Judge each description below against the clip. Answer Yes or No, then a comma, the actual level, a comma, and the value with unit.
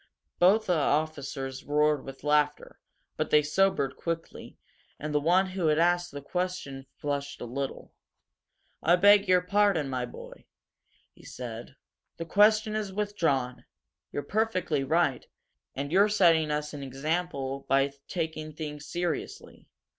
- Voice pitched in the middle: Yes, medium, 155 Hz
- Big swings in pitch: No, average, 4.4 semitones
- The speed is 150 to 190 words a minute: No, average, 140 wpm